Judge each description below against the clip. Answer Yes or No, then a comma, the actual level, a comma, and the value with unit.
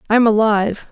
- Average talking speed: Yes, average, 195 wpm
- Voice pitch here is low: No, high, 215 Hz